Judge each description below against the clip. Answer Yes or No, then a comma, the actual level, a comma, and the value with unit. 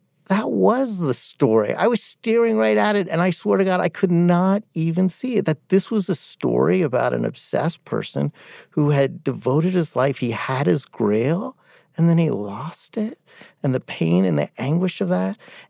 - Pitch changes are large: Yes, wide, 6.5 semitones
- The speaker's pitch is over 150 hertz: Yes, medium, 170 Hz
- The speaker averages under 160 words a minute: No, average, 200 wpm